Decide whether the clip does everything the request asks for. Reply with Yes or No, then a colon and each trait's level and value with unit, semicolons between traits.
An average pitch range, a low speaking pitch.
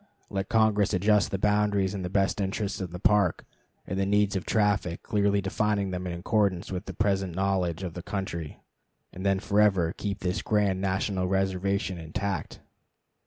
No: narrow, 1.9 semitones; very low, 95 Hz